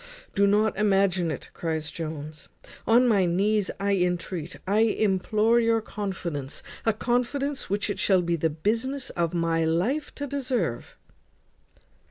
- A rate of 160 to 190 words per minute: No, average, 140 wpm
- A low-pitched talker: No, high, 195 Hz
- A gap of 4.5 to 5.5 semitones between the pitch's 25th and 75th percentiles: Yes, average, 4.9 semitones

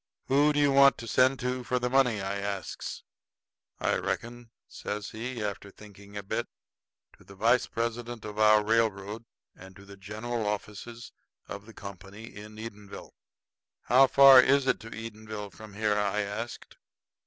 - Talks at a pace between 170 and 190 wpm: No, average, 160 wpm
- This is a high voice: No, low, 110 Hz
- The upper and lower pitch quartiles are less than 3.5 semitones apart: Yes, average, 2.9 semitones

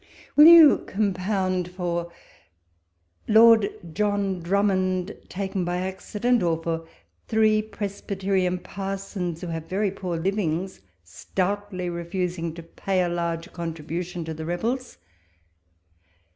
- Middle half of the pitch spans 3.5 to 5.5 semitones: No, average, 2.8 semitones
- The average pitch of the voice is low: No, medium, 185 Hz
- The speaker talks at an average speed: No, slow, 120 wpm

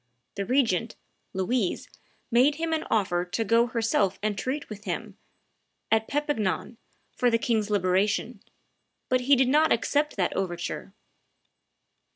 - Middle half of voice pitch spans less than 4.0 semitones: No, average, 4.6 semitones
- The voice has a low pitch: No, high, 225 Hz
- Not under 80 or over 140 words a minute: Yes, slow, 135 wpm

